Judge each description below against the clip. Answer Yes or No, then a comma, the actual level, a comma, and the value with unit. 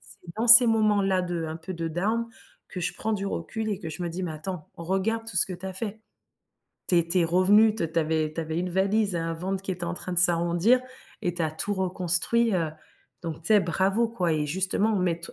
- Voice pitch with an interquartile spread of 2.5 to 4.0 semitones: Yes, average, 3.6 semitones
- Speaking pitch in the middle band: Yes, medium, 180 Hz